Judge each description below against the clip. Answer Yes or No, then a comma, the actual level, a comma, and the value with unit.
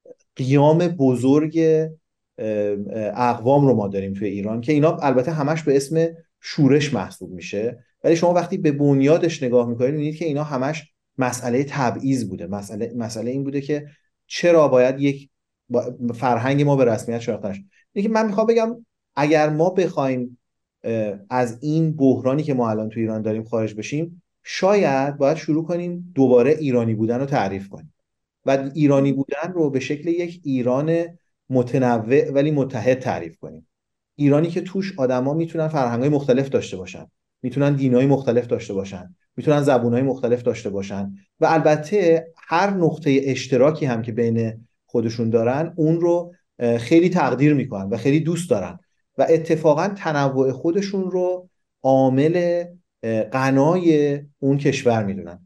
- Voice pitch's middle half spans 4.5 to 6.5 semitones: Yes, average, 4.8 semitones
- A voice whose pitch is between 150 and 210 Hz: No, medium, 140 Hz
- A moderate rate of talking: Yes, average, 145 wpm